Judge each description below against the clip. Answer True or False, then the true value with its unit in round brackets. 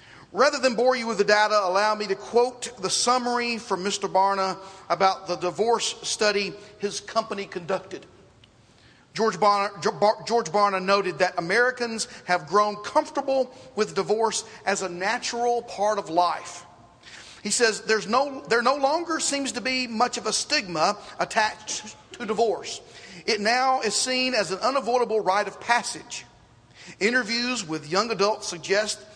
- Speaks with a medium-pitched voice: False (210 Hz)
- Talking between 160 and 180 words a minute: False (150 wpm)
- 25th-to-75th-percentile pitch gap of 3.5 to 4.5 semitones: True (3.8 semitones)